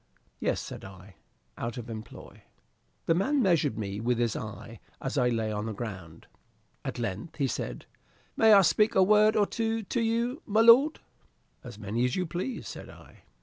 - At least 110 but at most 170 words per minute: No, average, 185 wpm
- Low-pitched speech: Yes, low, 130 Hz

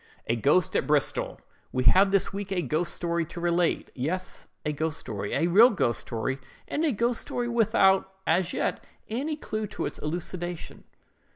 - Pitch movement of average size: Yes, average, 5.0 semitones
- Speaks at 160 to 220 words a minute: Yes, average, 170 wpm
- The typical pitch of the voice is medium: Yes, medium, 175 Hz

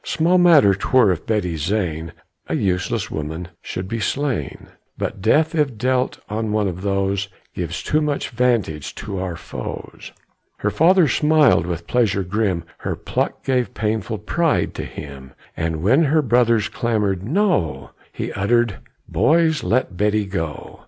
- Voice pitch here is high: No, low, 105 Hz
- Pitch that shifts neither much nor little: No, wide, 6.2 semitones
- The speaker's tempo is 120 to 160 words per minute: Yes, average, 150 wpm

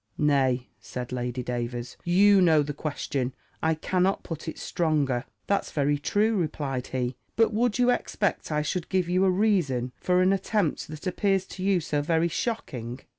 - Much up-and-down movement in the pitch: Yes, wide, 6.2 semitones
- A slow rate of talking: No, average, 175 wpm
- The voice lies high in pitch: No, medium, 160 Hz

